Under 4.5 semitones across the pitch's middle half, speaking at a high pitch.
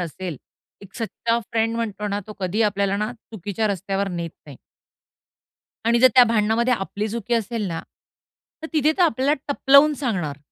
Yes: average, 3.3 semitones; high, 215 Hz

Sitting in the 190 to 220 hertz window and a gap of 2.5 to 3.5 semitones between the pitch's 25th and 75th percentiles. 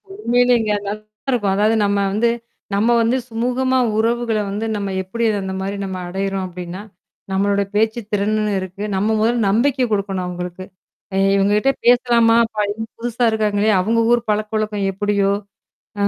Yes: high, 210 Hz; average, 2.9 semitones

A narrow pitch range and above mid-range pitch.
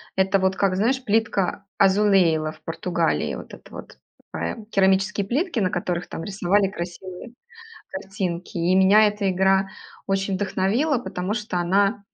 Yes: narrow, 2.1 semitones; high, 195 Hz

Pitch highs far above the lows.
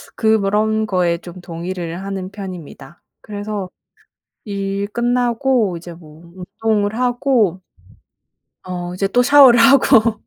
No: average, 3.8 semitones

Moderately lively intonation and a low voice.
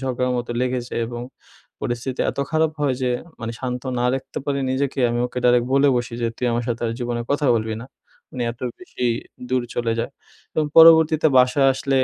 No: narrow, 2.3 semitones; low, 125 Hz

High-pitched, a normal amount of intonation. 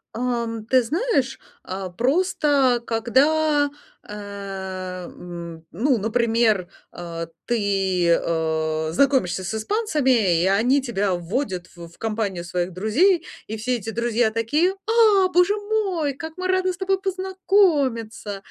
No: high, 230 Hz; wide, 8.3 semitones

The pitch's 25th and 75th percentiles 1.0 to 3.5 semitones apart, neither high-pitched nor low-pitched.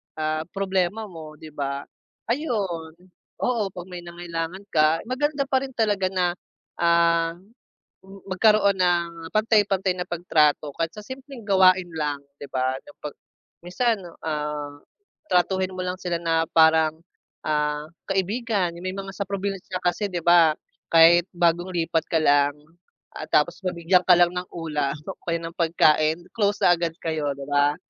Yes: average, 3.2 semitones; medium, 175 Hz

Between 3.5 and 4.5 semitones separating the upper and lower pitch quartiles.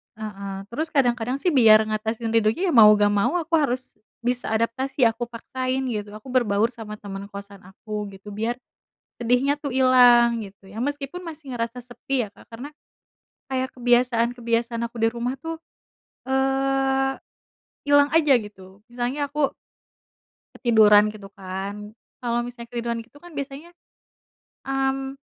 Yes: average, 3.8 semitones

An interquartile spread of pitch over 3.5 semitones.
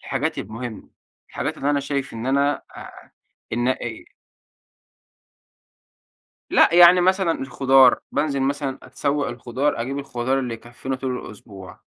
No: average, 2.8 semitones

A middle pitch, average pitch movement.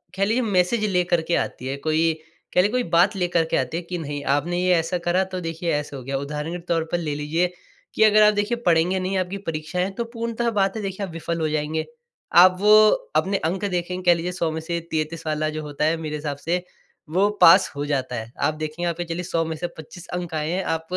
Yes: medium, 170 Hz; average, 3.0 semitones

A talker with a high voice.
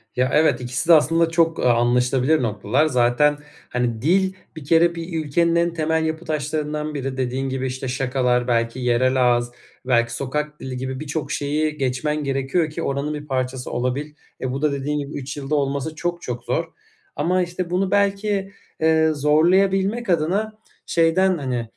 No: medium, 150 Hz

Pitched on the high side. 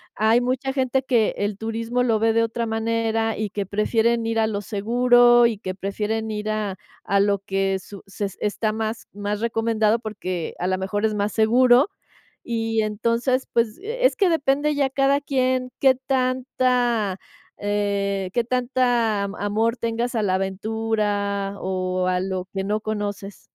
Yes: high, 220 Hz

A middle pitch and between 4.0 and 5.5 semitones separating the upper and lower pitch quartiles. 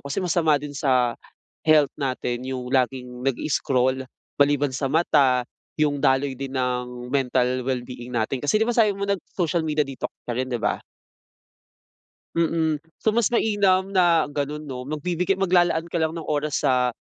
Yes: medium, 145 Hz; average, 4.6 semitones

